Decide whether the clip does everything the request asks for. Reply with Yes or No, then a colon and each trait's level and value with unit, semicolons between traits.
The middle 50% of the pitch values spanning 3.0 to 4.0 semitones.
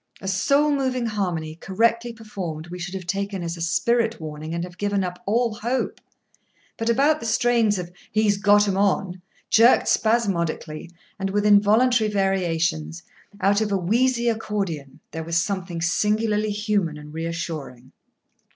No: average, 4.7 semitones